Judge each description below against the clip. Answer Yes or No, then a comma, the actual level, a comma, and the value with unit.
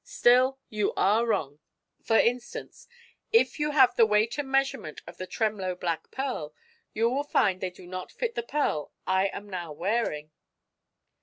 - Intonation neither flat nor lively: No, wide, 5.9 semitones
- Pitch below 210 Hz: No, high, 215 Hz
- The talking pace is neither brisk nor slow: Yes, average, 165 wpm